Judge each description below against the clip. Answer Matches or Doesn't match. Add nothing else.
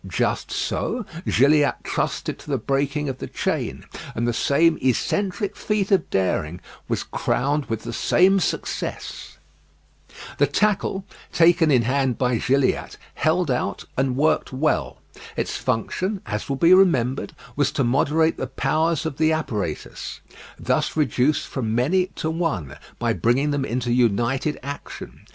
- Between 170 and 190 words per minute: Doesn't match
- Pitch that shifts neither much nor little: Matches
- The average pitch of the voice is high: Doesn't match